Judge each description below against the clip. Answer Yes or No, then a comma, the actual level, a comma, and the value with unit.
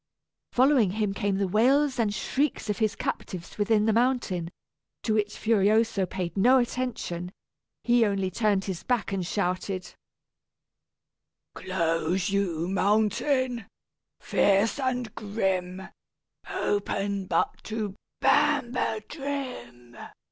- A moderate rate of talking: No, slow, 105 wpm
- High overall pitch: Yes, high, 210 Hz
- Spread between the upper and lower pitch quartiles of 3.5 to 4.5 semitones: Yes, average, 4.2 semitones